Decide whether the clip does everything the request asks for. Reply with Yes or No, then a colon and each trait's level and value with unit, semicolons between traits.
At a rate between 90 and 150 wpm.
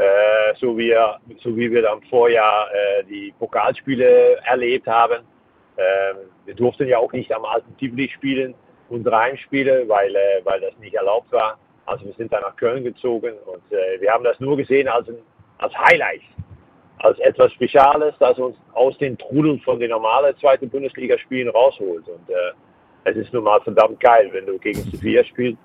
No: average, 180 wpm